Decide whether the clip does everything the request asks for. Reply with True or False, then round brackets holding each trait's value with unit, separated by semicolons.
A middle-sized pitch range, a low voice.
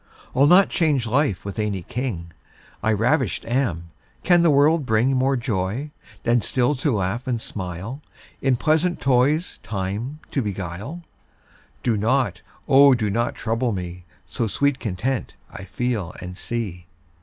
False (5.7 semitones; 120 Hz)